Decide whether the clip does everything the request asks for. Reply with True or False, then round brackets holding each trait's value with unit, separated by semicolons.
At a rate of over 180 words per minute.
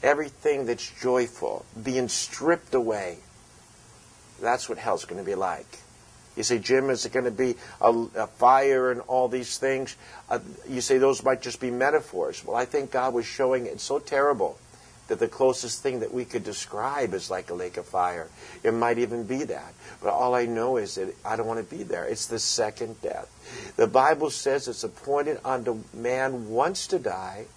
True (195 wpm)